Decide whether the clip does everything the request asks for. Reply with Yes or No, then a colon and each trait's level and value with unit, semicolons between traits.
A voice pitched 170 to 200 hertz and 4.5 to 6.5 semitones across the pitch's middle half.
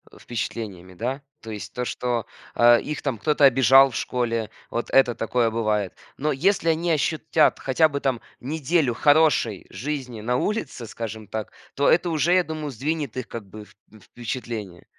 No: low, 125 Hz; average, 4.9 semitones